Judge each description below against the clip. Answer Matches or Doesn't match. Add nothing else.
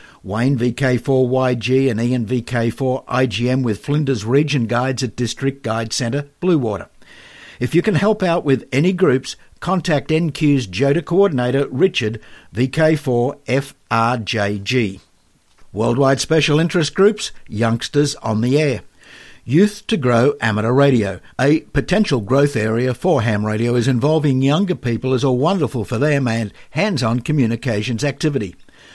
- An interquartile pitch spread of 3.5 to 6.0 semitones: Matches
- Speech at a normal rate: Doesn't match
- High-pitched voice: Doesn't match